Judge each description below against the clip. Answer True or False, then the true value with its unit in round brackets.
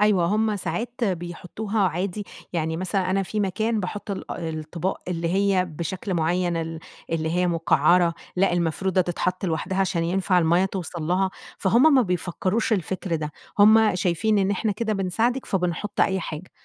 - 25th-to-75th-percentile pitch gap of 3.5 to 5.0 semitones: False (3.0 semitones)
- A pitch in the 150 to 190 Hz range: True (185 Hz)